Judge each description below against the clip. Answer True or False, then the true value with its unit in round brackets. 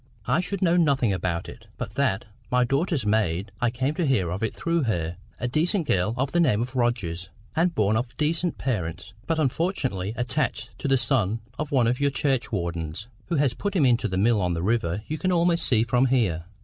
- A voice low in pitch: True (120 Hz)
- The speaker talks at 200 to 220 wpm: True (205 wpm)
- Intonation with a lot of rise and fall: True (7.0 semitones)